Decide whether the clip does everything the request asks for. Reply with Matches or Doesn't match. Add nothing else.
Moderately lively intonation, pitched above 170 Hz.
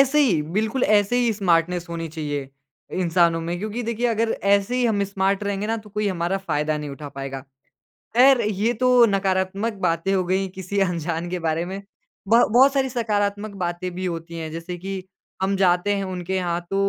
Matches